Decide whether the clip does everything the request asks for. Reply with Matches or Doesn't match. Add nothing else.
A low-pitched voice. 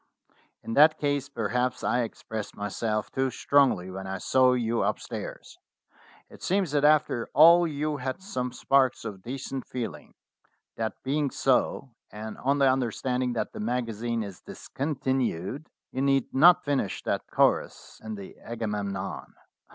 Matches